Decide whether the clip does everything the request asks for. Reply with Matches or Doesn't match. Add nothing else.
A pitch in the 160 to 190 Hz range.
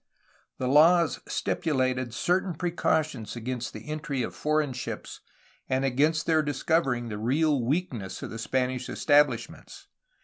Doesn't match